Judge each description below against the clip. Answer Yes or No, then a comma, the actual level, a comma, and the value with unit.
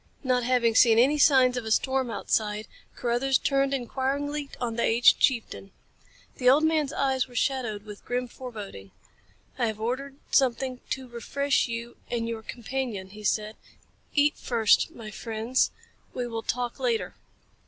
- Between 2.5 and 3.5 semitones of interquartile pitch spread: Yes, average, 2.9 semitones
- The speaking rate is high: No, average, 155 wpm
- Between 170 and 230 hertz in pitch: No, high, 245 Hz